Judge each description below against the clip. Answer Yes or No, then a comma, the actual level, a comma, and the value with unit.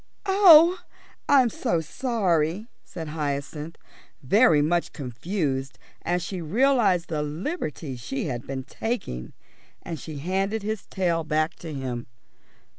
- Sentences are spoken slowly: Yes, slow, 120 wpm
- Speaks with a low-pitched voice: No, medium, 165 Hz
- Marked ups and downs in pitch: Yes, wide, 6.2 semitones